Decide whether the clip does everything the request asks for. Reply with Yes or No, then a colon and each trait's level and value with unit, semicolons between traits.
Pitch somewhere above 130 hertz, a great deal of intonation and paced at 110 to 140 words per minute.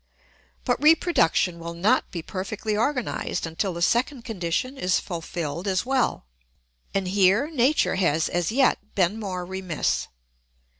Yes: high, 190 Hz; wide, 6.0 semitones; slow, 135 wpm